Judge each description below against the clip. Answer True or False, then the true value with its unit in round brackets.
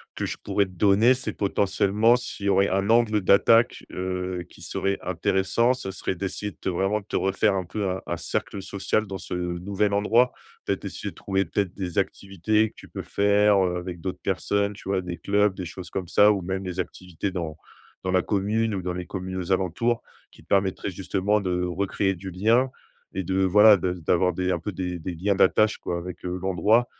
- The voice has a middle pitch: False (95 Hz)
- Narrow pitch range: True (2.1 semitones)